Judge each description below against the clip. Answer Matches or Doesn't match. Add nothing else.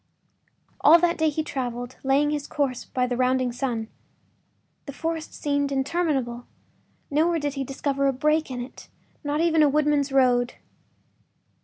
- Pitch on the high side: Matches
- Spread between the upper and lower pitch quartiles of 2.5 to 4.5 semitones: Matches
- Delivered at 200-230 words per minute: Doesn't match